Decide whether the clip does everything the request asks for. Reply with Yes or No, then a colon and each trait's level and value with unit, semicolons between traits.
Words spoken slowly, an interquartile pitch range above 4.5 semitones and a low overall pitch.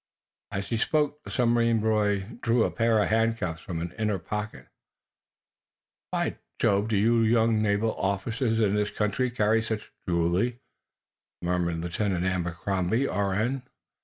No: slow, 130 wpm; average, 2.9 semitones; low, 105 Hz